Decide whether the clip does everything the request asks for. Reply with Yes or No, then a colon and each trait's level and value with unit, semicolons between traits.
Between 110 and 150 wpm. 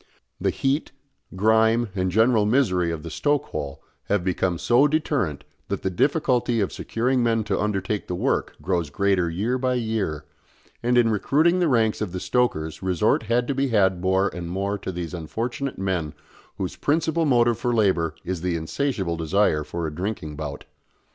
No: average, 175 wpm